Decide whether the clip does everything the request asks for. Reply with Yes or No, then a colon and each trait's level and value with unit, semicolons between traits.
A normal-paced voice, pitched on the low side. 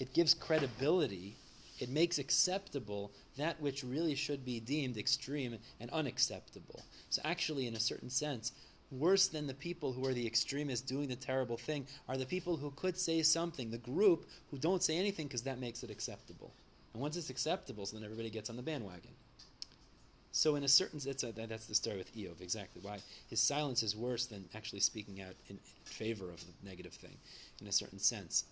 Yes: average, 195 wpm; low, 130 Hz